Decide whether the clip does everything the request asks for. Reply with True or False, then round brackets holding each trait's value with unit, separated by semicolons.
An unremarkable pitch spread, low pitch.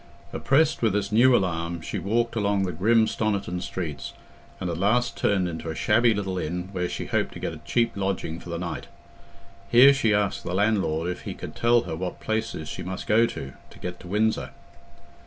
True (4.0 semitones; 100 Hz)